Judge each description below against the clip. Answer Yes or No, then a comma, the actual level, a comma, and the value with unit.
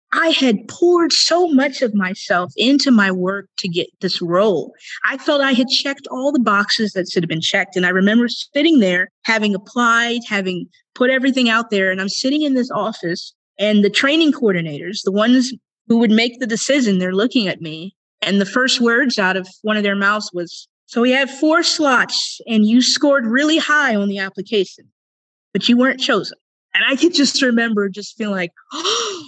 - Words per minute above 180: Yes, average, 200 wpm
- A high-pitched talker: Yes, high, 230 Hz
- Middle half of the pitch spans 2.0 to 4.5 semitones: No, average, 5.3 semitones